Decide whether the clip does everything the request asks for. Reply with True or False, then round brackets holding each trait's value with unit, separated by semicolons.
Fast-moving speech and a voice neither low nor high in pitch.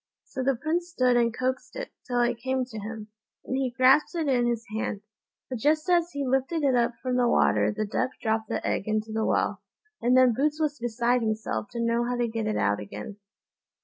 False (220 wpm; 245 Hz)